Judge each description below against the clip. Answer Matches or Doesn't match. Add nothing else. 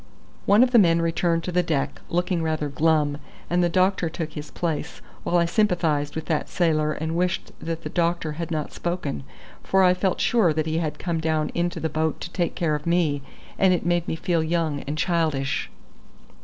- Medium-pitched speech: Matches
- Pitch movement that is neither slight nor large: Doesn't match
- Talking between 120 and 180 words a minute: Doesn't match